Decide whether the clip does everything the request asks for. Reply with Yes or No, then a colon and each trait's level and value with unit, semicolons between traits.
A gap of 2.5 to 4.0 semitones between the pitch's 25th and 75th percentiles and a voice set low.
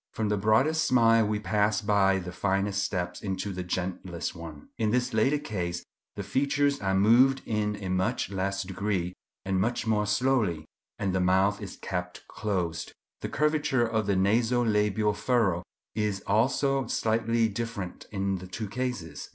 Yes: average, 3.3 semitones; low, 105 Hz